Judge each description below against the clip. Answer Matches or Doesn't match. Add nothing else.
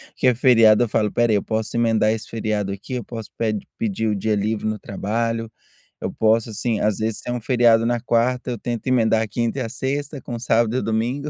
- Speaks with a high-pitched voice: Doesn't match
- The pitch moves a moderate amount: Doesn't match